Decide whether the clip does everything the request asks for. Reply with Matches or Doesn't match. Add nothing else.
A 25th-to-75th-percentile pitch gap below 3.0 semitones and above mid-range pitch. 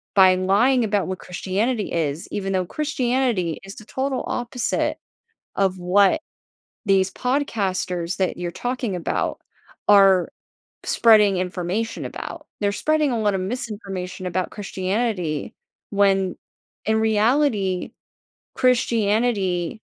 Doesn't match